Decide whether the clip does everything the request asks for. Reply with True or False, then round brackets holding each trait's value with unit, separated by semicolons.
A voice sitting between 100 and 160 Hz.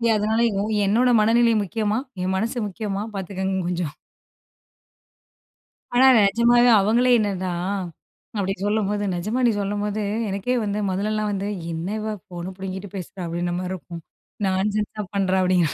False (200 Hz)